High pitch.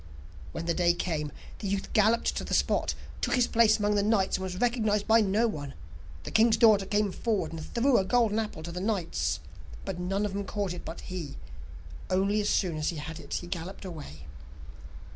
Yes: high, 195 Hz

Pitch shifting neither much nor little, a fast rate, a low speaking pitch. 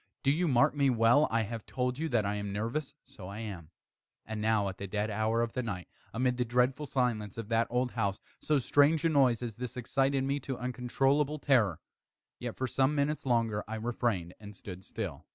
Yes: average, 4.0 semitones; fast, 210 wpm; low, 120 Hz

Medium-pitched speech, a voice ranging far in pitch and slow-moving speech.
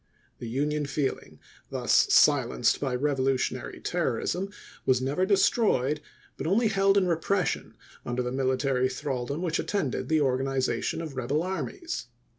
Yes: medium, 145 Hz; wide, 5.8 semitones; slow, 130 wpm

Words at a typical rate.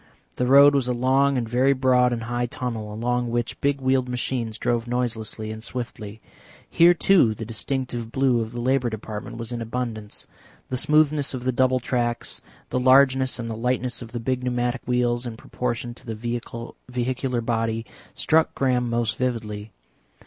Yes: average, 170 wpm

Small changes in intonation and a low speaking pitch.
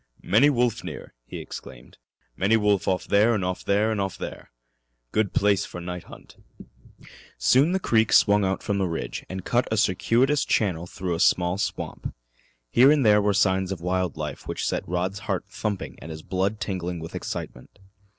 No: average, 3.2 semitones; low, 100 Hz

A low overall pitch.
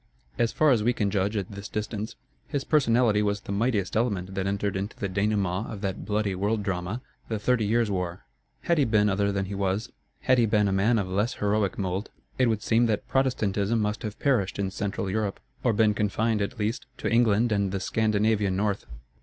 Yes: low, 105 Hz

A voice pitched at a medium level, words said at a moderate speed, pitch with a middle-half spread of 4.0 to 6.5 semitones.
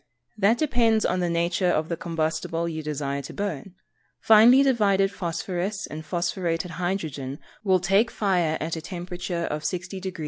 No: medium, 175 Hz; average, 165 wpm; average, 3.2 semitones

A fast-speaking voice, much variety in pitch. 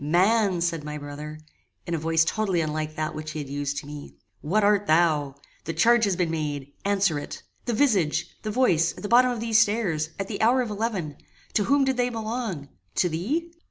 Yes: fast, 210 wpm; wide, 6.3 semitones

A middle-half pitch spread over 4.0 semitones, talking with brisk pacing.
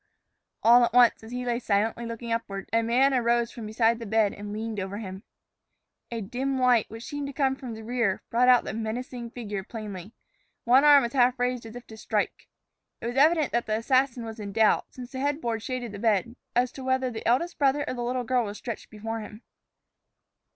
No: narrow, 2.4 semitones; fast, 215 wpm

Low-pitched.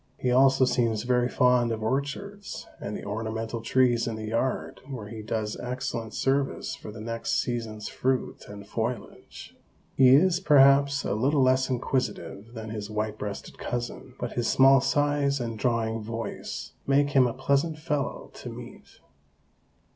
Yes: low, 125 Hz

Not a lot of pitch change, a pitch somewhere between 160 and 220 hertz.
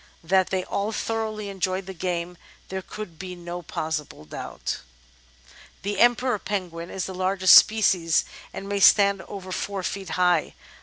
Yes: narrow, 2.2 semitones; high, 190 Hz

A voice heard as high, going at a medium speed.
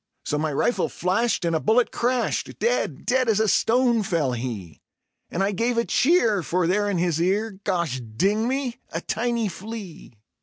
Yes: high, 205 Hz; average, 180 wpm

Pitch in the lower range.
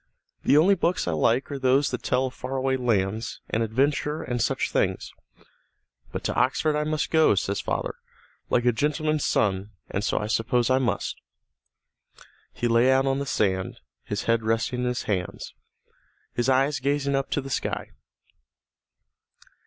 Yes: low, 130 Hz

